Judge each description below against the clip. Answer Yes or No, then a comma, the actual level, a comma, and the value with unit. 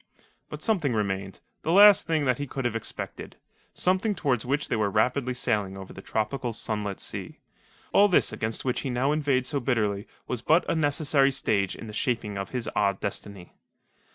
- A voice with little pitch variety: No, wide, 5.6 semitones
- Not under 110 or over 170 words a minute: No, average, 185 wpm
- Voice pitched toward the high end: No, low, 125 Hz